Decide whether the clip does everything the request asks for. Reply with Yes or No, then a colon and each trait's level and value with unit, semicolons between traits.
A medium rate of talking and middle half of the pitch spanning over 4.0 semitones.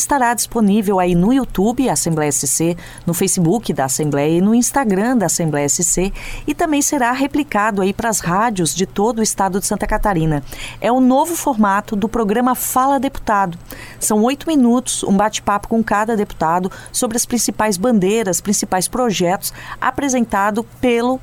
Yes: average, 160 wpm; average, 5.0 semitones